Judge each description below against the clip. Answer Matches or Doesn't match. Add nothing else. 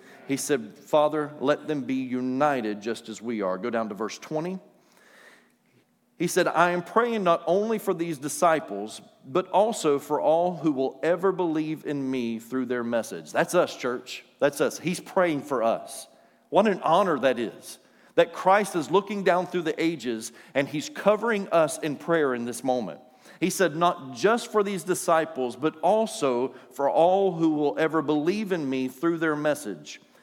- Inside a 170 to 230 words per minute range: Matches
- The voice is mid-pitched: Matches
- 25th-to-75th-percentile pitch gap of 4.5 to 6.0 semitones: Matches